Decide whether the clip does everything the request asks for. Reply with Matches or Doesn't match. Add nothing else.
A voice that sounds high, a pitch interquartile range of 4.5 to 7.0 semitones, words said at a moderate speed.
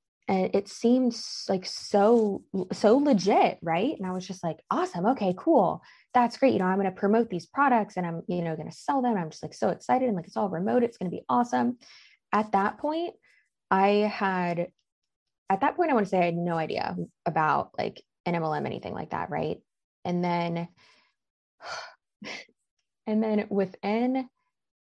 Matches